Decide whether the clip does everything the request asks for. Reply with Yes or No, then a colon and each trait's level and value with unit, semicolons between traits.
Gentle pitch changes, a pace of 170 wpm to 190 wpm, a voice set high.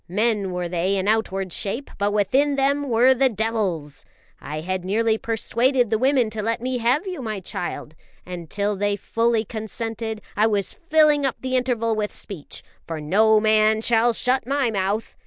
No: average, 3.7 semitones; average, 175 wpm; high, 220 Hz